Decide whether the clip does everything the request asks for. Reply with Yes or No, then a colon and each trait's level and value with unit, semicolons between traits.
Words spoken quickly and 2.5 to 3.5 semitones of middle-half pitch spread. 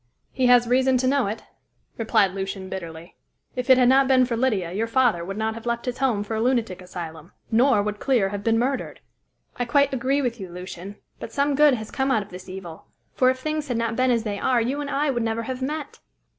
No: fast, 240 wpm; average, 4.4 semitones